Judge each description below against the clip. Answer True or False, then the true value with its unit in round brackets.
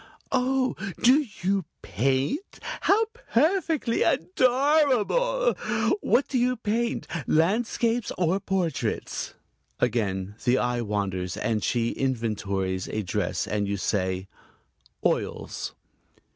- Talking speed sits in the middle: False (100 wpm)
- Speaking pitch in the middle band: True (180 Hz)